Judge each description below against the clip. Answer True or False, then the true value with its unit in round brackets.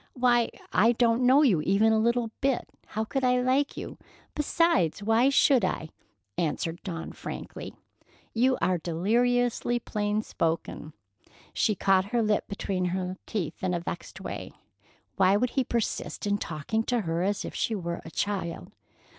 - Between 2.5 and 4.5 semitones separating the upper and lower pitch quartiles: False (5.0 semitones)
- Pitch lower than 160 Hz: False (210 Hz)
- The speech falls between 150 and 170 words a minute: True (160 wpm)